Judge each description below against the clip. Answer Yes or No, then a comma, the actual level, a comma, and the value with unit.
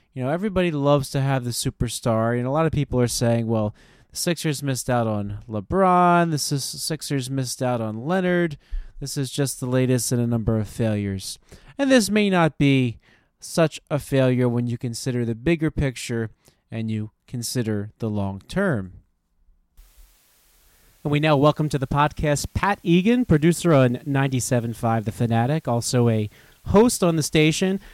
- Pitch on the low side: Yes, low, 130 Hz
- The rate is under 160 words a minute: No, average, 170 wpm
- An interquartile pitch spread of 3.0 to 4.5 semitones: No, average, 5.1 semitones